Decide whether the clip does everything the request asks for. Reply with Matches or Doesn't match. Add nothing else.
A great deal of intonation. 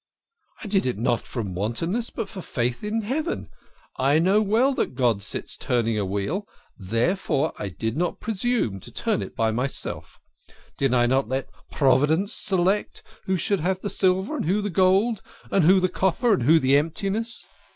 Matches